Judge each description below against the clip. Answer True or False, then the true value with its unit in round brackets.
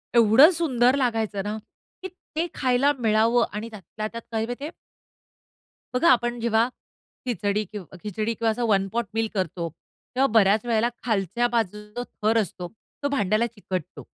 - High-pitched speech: True (225 Hz)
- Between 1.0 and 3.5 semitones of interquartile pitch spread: True (2.6 semitones)